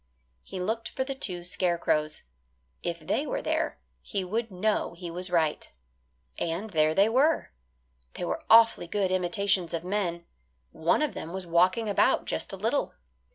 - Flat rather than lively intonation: No, average, 4.1 semitones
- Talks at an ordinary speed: Yes, average, 160 wpm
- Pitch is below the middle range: No, medium, 185 Hz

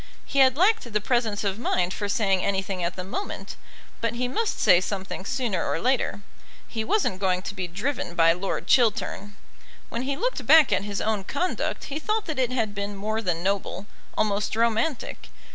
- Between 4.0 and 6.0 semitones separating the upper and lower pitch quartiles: Yes, average, 5.0 semitones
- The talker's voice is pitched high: Yes, high, 210 Hz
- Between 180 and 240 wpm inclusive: Yes, average, 190 wpm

